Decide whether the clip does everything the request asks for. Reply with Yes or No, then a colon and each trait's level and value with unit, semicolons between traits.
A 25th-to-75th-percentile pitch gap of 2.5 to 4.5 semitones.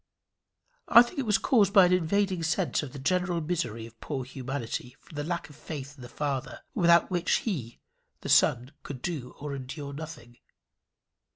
No: average, 5.2 semitones